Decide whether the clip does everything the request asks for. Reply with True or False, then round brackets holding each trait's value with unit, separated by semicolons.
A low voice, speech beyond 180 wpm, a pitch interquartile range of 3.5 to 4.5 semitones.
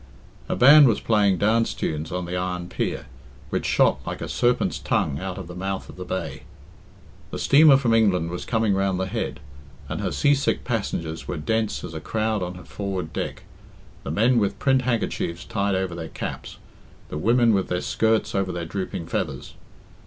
True (95 Hz; 190 wpm; 4.1 semitones)